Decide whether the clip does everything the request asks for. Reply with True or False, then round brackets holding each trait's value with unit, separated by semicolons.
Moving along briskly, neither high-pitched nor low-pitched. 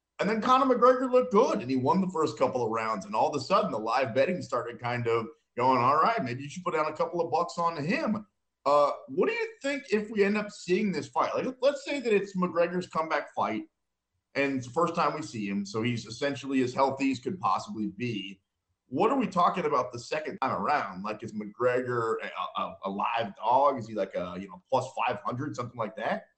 True (240 wpm; 150 Hz)